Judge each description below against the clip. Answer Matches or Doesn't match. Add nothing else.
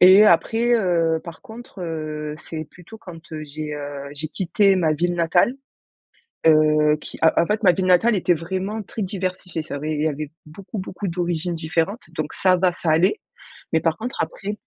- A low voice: Doesn't match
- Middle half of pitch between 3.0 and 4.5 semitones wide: Matches